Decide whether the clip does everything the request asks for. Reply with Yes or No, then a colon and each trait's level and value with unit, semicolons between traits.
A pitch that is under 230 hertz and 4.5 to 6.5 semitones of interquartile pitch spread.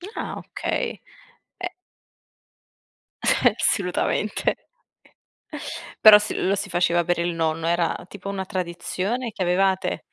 No: medium, 185 Hz; narrow, 2.5 semitones